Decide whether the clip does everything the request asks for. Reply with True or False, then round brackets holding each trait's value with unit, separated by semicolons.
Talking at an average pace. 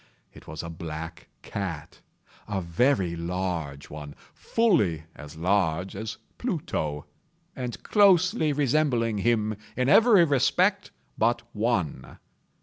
False (100 wpm)